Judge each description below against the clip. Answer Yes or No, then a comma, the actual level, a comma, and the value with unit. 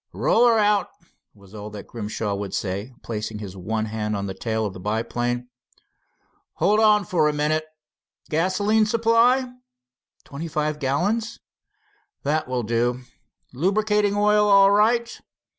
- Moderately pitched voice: Yes, medium, 150 Hz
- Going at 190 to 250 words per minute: No, average, 140 wpm